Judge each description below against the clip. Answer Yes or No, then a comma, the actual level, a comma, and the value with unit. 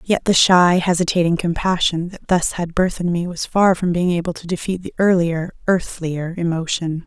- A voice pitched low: No, medium, 175 Hz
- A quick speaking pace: No, average, 185 wpm